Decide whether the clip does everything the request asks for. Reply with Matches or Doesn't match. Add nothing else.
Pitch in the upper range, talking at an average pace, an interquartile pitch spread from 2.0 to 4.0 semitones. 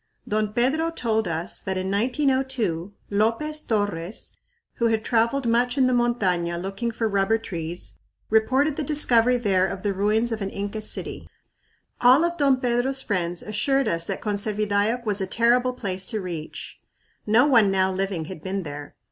Doesn't match